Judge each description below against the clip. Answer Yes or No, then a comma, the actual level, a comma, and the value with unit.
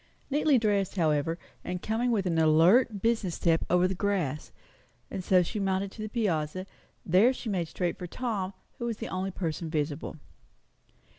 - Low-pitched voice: No, medium, 185 Hz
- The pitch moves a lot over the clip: No, average, 4.3 semitones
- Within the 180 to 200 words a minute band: No, average, 170 wpm